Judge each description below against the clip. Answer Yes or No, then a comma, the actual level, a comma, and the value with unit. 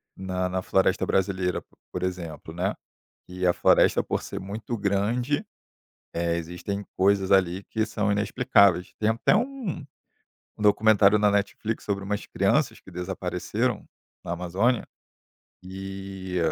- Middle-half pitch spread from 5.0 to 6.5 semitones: No, narrow, 2.5 semitones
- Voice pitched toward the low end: Yes, very low, 95 Hz